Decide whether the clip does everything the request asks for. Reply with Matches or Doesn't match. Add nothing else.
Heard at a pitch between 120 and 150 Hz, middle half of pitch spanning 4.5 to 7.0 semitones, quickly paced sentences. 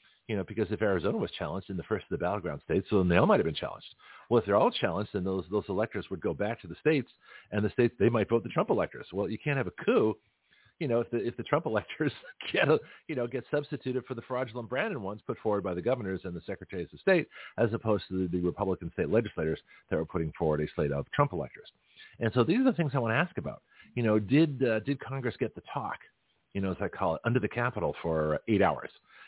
Doesn't match